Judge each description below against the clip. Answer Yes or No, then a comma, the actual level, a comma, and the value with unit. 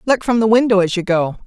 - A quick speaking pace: Yes, fast, 285 wpm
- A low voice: No, high, 205 Hz